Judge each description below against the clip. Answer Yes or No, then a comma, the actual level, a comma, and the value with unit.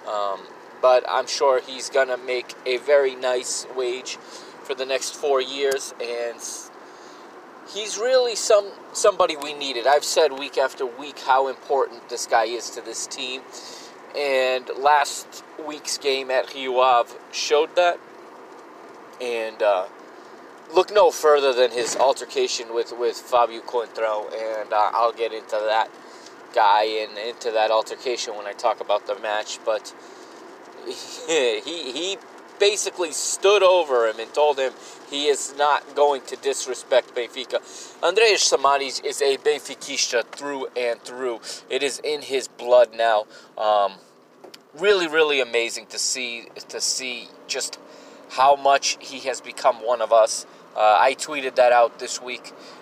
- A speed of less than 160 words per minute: Yes, average, 145 wpm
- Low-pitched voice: No, medium, 145 Hz